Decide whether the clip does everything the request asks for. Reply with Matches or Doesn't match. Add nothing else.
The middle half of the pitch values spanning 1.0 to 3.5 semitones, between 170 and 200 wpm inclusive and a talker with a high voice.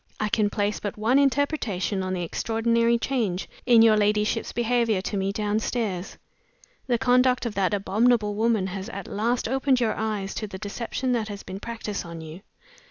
Matches